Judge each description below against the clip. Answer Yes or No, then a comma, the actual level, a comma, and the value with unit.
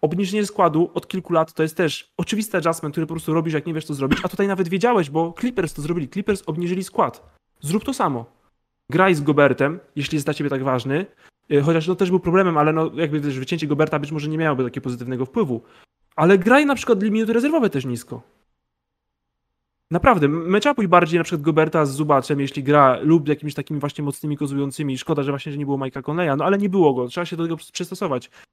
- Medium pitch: Yes, medium, 160 Hz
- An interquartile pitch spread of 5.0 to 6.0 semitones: No, average, 4.4 semitones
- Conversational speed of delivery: No, fast, 220 wpm